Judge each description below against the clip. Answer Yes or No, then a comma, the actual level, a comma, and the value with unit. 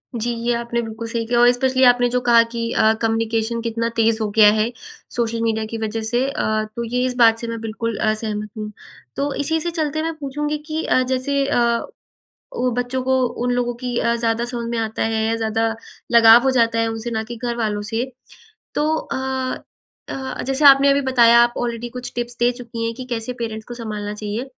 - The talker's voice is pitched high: Yes, high, 235 Hz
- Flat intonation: Yes, narrow, 1.9 semitones